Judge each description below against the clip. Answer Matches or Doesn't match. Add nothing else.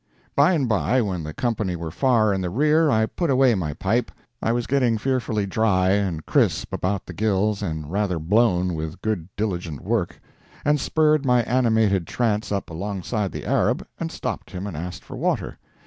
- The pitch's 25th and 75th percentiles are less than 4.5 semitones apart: Doesn't match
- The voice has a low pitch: Matches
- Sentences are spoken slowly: Doesn't match